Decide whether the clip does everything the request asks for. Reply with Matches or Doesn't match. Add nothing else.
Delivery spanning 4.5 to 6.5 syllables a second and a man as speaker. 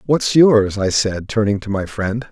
Doesn't match